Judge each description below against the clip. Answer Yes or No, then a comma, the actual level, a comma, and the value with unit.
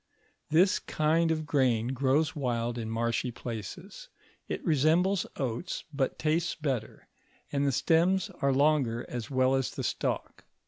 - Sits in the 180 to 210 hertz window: No, medium, 140 Hz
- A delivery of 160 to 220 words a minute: No, average, 140 wpm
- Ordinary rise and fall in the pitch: Yes, average, 4.6 semitones